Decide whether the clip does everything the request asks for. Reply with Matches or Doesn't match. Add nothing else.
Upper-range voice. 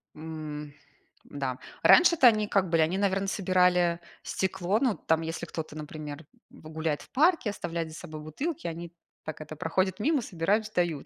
Doesn't match